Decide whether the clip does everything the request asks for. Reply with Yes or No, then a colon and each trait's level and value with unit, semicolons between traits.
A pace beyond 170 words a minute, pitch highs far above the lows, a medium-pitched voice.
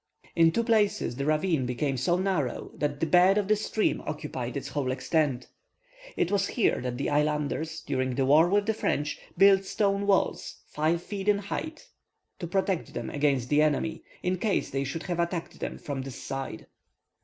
Yes: average, 185 wpm; wide, 5.8 semitones; medium, 160 Hz